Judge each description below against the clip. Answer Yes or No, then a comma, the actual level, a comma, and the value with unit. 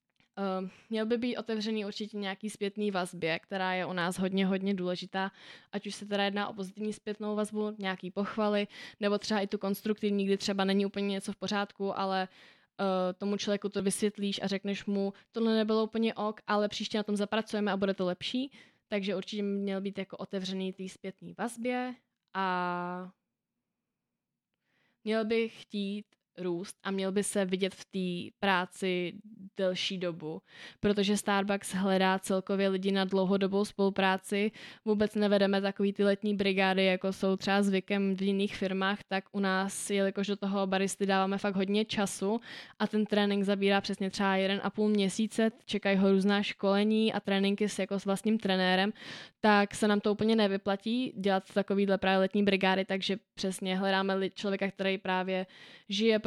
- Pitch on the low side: No, high, 200 Hz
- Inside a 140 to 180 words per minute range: Yes, average, 165 wpm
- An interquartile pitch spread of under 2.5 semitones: Yes, narrow, 1.4 semitones